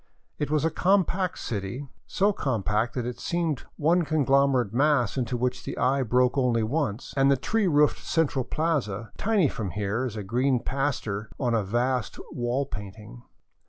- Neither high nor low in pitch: No, low, 130 Hz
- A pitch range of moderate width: Yes, average, 4.4 semitones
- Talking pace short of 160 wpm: No, average, 175 wpm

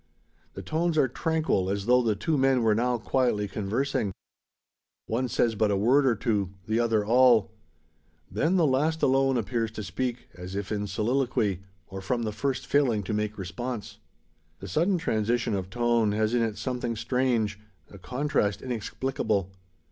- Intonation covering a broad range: No, average, 3.9 semitones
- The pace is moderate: Yes, average, 165 wpm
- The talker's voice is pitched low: Yes, low, 115 Hz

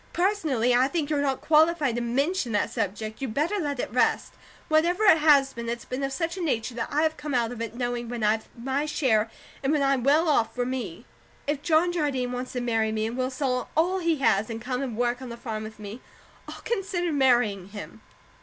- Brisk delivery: Yes, fast, 230 wpm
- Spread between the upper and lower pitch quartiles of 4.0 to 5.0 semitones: Yes, average, 4.6 semitones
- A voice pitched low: No, very high, 255 Hz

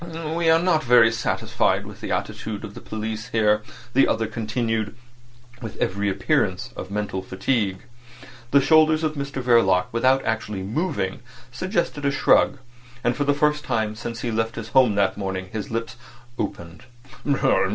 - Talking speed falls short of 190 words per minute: Yes, average, 160 wpm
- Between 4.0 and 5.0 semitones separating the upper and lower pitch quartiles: Yes, average, 4.6 semitones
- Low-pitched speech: Yes, low, 115 Hz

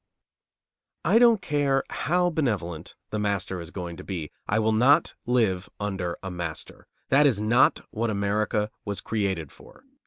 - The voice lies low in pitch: Yes, low, 105 Hz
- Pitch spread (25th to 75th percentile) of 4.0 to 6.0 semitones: Yes, average, 5.3 semitones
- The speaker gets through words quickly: No, average, 155 wpm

